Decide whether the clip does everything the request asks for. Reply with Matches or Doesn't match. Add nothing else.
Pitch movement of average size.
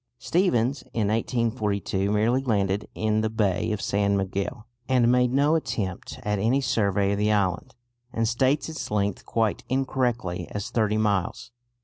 Matches